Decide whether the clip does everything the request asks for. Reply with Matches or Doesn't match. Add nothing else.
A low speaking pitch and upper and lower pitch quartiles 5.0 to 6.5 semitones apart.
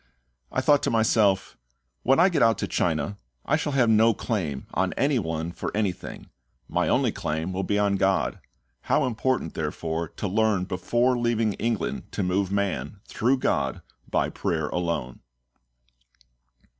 Matches